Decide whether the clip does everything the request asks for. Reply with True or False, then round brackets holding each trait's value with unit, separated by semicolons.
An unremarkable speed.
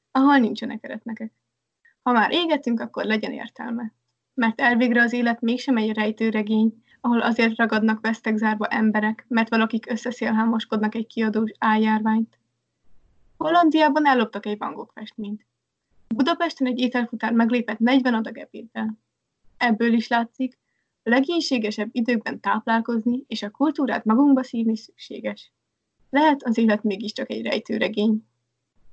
True (120 wpm)